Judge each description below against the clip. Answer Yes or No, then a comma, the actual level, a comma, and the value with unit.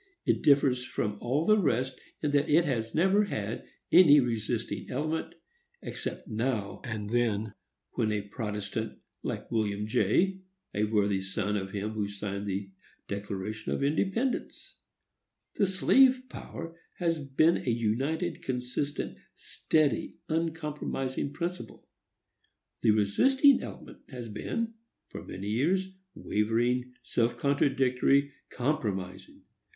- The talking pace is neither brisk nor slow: No, slow, 115 wpm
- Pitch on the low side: Yes, low, 125 Hz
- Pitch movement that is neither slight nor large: No, wide, 6.7 semitones